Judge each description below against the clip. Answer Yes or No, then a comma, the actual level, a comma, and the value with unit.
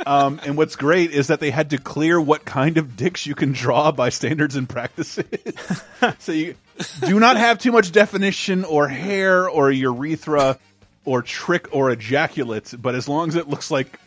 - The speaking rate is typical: Yes, average, 190 wpm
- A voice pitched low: No, medium, 150 Hz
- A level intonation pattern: No, average, 4.0 semitones